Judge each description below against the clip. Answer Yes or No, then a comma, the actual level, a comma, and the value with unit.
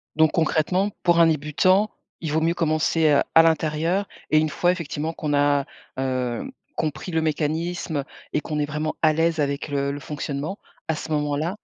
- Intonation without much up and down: Yes, narrow, 2.0 semitones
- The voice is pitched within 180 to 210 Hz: No, medium, 155 Hz